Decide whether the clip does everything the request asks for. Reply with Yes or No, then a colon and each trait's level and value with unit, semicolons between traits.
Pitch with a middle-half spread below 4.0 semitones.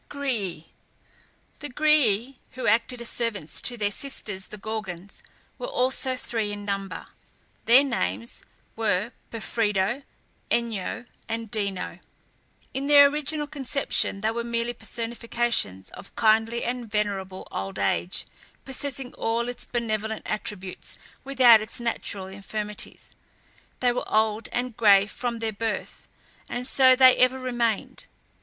Yes: average, 3.4 semitones